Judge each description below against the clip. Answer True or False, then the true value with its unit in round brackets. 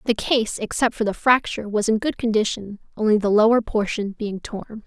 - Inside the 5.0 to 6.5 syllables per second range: True (5.3 syllables/s)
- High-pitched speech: True (220 Hz)